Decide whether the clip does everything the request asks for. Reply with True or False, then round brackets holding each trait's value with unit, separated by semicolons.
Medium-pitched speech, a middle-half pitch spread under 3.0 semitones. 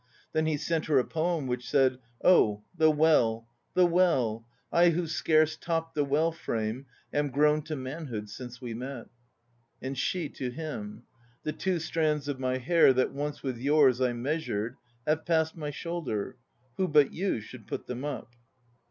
False (145 Hz; 4.2 semitones)